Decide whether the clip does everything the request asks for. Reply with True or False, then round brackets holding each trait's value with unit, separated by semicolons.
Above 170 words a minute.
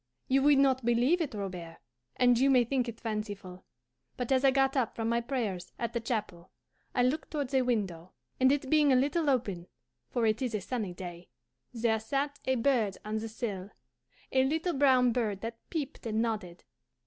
True (195 wpm)